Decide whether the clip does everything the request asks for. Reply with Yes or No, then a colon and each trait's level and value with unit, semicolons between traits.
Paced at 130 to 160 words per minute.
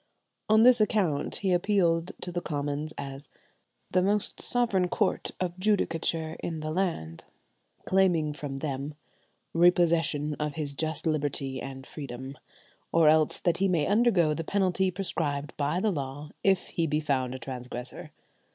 Yes: average, 150 wpm